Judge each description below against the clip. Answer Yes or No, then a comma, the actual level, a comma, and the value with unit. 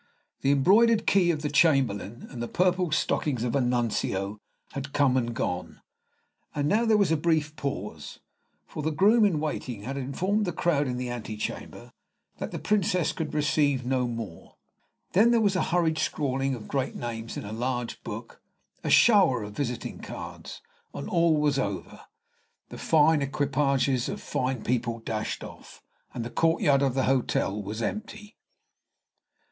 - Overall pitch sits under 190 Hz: Yes, medium, 140 Hz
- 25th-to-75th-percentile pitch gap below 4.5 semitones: No, average, 5.2 semitones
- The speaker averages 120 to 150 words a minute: No, average, 165 wpm